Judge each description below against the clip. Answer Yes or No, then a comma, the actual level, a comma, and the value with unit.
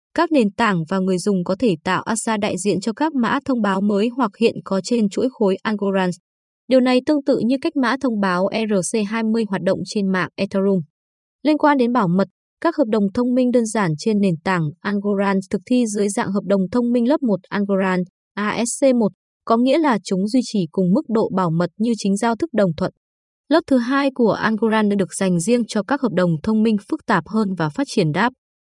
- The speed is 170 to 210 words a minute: No, average, 220 wpm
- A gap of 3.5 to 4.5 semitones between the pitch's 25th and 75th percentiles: Yes, average, 4.2 semitones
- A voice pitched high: Yes, high, 215 Hz